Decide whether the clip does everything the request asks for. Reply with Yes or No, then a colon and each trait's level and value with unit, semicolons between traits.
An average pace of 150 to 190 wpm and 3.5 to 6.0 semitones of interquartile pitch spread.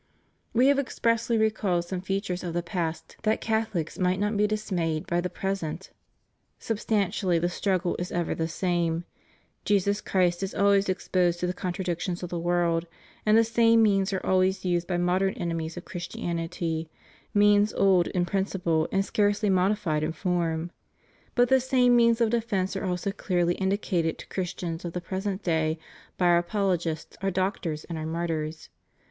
No: average, 170 wpm; average, 2.9 semitones